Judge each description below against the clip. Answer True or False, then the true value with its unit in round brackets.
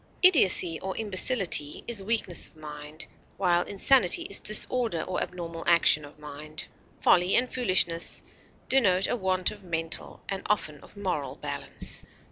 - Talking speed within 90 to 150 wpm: True (140 wpm)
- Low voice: False (180 Hz)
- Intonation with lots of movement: False (3.9 semitones)